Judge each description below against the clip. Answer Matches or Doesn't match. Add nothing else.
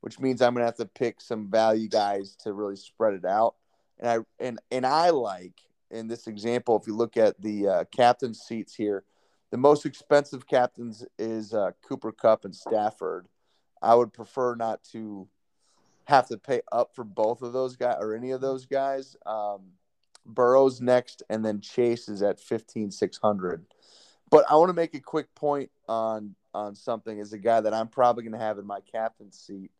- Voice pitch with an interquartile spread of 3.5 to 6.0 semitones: Doesn't match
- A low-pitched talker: Matches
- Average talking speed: Matches